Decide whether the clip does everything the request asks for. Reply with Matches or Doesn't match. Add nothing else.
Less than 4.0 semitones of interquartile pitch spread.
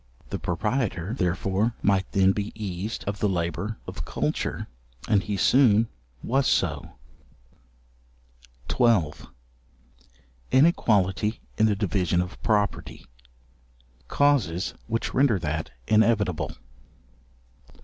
Matches